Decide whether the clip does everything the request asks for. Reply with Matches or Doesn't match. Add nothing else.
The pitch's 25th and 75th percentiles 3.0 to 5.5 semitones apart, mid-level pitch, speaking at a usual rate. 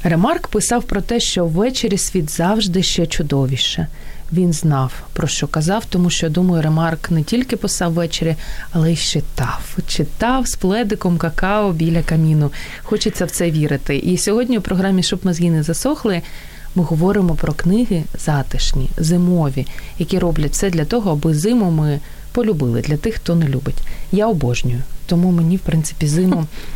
Doesn't match